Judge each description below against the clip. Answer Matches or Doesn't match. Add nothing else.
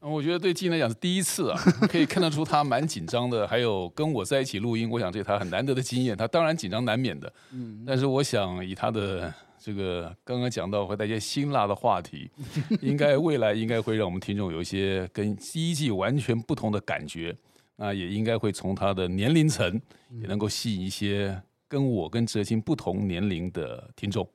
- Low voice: Matches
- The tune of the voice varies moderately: Doesn't match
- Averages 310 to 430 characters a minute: Matches